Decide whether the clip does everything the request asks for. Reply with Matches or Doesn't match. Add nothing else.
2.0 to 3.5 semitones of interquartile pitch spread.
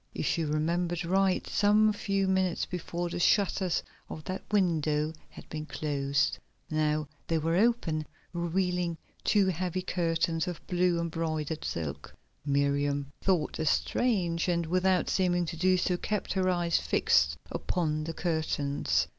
Matches